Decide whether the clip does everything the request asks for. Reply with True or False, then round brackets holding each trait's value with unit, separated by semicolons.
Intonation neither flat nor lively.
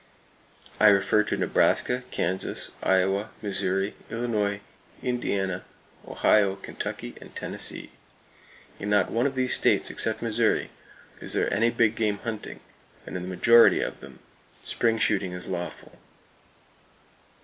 True (3.0 semitones)